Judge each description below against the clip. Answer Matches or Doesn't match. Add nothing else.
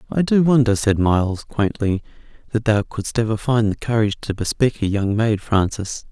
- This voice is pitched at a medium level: Doesn't match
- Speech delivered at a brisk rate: Doesn't match